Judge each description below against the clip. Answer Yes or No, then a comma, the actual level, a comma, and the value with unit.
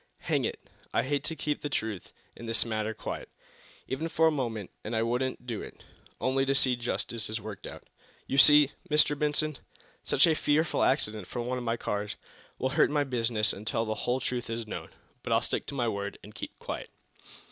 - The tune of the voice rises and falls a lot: No, average, 4.3 semitones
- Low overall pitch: Yes, low, 120 Hz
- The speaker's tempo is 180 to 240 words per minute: Yes, average, 200 wpm